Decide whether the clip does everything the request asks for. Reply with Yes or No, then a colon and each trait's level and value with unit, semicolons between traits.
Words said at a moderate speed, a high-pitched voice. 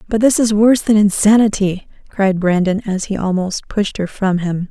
Yes: average, 190 wpm; high, 200 Hz